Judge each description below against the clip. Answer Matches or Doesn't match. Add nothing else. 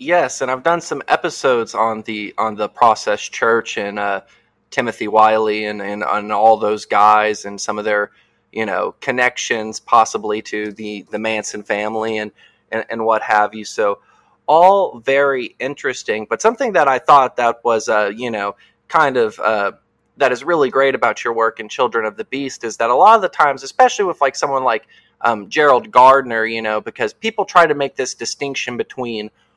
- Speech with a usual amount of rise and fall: Matches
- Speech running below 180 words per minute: Doesn't match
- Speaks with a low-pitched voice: Matches